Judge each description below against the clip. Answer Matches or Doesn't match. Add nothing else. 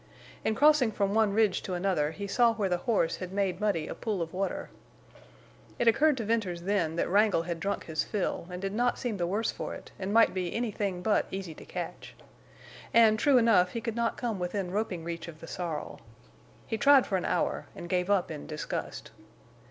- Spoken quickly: Matches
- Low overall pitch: Doesn't match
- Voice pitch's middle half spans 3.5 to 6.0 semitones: Matches